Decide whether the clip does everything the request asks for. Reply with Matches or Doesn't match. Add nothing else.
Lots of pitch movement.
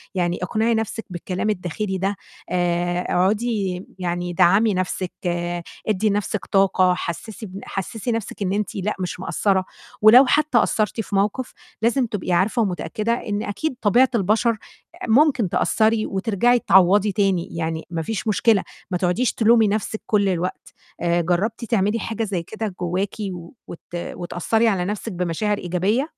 Doesn't match